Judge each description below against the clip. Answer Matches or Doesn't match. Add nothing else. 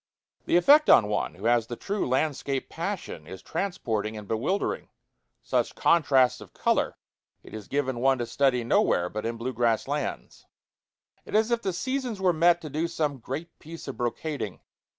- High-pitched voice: Doesn't match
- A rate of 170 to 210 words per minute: Matches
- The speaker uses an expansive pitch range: Matches